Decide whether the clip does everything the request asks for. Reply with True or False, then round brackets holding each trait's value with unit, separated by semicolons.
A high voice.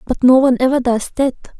True (255 Hz)